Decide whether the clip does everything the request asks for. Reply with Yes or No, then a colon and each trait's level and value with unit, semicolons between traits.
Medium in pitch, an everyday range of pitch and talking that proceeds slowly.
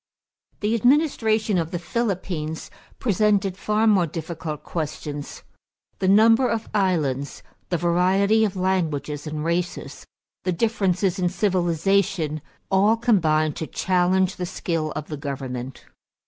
Yes: medium, 180 Hz; average, 4.6 semitones; slow, 125 wpm